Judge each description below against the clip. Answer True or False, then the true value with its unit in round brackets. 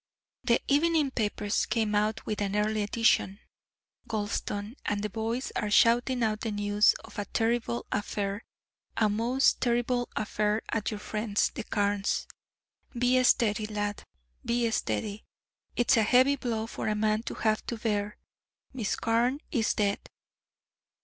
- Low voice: False (220 Hz)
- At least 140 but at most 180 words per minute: True (145 wpm)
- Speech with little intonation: True (2.2 semitones)